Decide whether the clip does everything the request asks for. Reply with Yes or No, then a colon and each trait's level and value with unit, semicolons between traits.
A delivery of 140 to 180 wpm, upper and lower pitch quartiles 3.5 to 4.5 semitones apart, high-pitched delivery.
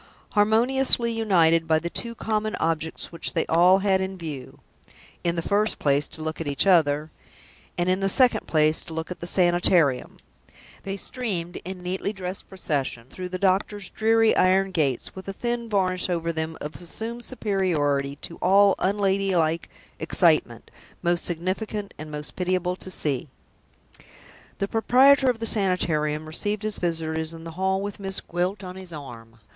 No: average, 165 wpm; average, 3.8 semitones; medium, 180 Hz